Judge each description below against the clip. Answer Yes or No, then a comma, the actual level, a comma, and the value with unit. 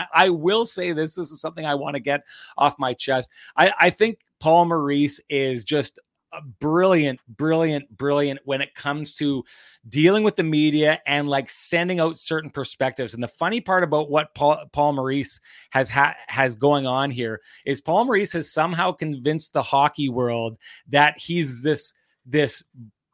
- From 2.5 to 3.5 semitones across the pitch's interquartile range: Yes, average, 3.0 semitones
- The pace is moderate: Yes, average, 175 wpm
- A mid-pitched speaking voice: Yes, medium, 145 Hz